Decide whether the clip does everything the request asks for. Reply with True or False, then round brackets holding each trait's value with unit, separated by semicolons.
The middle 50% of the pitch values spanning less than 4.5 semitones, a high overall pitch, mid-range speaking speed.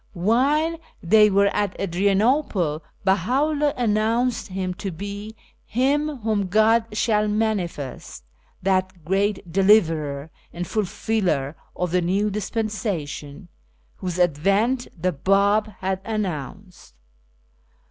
False (3.6 semitones; 200 Hz; 105 wpm)